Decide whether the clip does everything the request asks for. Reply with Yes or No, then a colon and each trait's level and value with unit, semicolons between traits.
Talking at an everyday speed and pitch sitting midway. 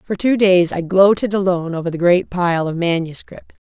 Yes: average, 195 wpm; medium, 180 Hz